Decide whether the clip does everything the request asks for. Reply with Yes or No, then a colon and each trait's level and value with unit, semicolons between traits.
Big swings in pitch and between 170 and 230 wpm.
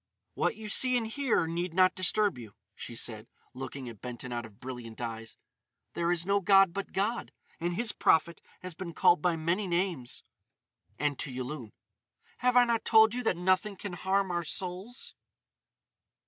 Yes: wide, 7.4 semitones; average, 175 wpm